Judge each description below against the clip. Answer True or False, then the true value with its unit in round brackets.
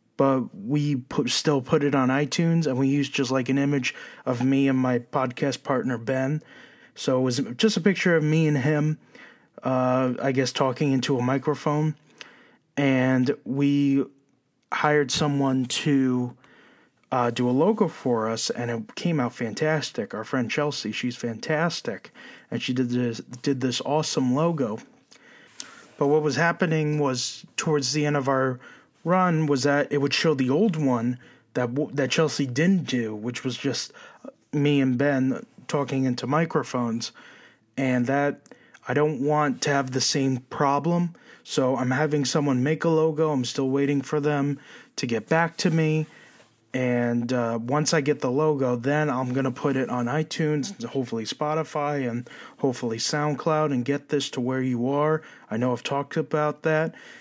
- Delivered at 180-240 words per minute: False (170 wpm)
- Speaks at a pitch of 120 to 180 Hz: True (140 Hz)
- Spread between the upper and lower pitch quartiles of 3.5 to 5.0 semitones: False (2.9 semitones)